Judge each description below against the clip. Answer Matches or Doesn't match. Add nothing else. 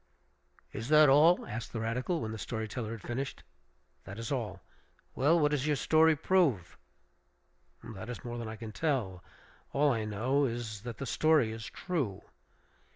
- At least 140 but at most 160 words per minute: Doesn't match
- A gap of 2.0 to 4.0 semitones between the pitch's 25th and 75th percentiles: Doesn't match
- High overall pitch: Doesn't match